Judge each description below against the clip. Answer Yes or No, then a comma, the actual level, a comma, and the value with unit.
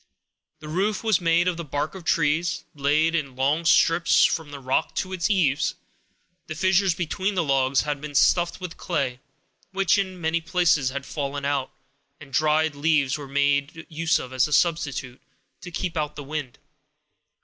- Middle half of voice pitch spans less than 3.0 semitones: No, average, 3.3 semitones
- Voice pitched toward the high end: No, medium, 155 Hz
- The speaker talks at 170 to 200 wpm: Yes, average, 175 wpm